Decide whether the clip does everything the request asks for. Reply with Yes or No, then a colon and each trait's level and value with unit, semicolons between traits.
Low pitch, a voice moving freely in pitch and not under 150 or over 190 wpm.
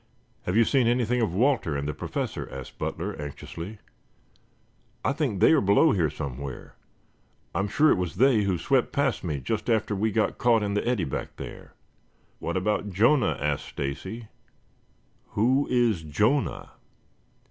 Yes: low, 105 Hz; wide, 5.8 semitones; average, 160 wpm